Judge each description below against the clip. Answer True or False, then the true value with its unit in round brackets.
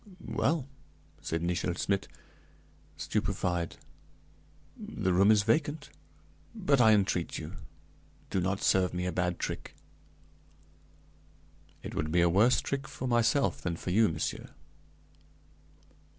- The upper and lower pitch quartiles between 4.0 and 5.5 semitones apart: True (5.1 semitones)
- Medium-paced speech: False (120 wpm)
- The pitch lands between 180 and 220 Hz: False (95 Hz)